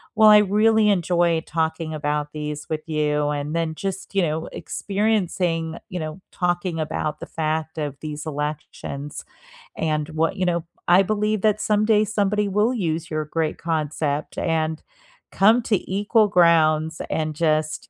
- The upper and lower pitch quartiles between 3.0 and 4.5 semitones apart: Yes, average, 4.2 semitones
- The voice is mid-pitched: Yes, medium, 165 Hz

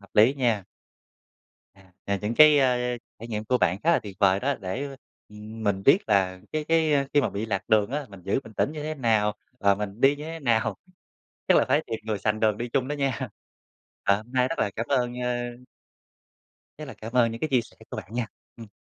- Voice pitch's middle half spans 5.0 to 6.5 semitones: No, average, 4.6 semitones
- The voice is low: Yes, low, 115 Hz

